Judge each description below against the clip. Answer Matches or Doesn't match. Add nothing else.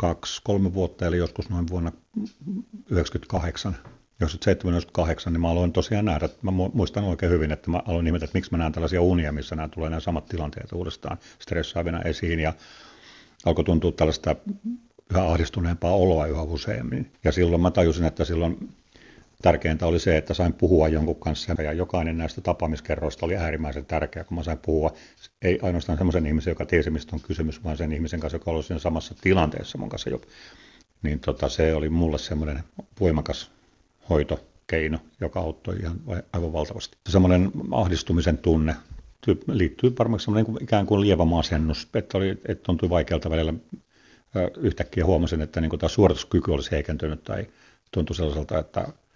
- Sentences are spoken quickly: Matches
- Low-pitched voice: Matches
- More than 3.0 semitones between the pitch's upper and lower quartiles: Doesn't match